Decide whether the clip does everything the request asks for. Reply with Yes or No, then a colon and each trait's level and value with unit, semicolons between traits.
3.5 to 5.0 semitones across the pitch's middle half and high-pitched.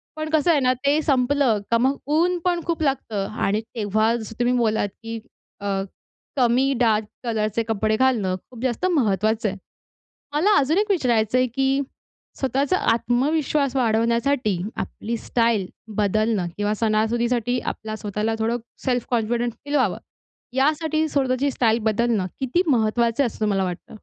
Yes: average, 4.0 semitones; high, 235 Hz